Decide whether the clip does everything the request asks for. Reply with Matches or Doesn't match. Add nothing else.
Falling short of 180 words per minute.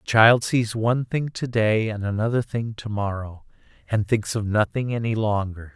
Doesn't match